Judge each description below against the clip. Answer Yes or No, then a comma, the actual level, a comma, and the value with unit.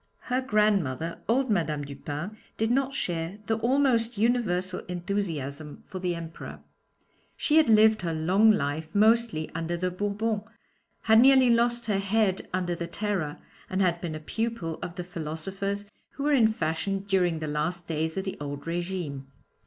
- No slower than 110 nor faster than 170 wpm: Yes, average, 160 wpm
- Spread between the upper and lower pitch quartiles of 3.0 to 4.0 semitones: No, average, 5.1 semitones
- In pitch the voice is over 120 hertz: Yes, high, 190 Hz